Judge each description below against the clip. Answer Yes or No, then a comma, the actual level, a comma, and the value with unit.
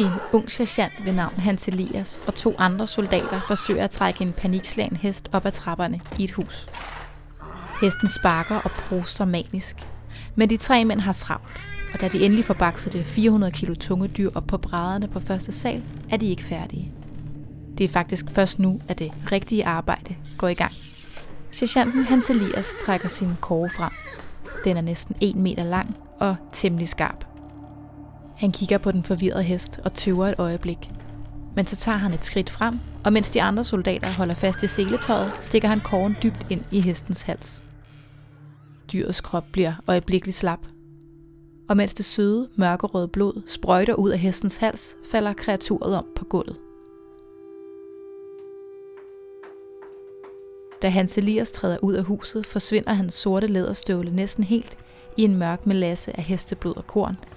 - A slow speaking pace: No, average, 165 wpm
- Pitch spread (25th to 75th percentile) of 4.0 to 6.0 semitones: No, average, 3.5 semitones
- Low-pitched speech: No, high, 190 Hz